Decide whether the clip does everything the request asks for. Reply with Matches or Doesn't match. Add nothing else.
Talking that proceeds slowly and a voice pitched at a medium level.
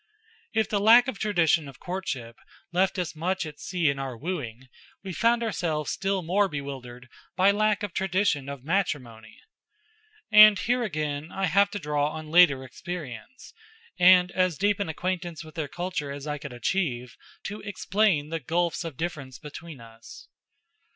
Doesn't match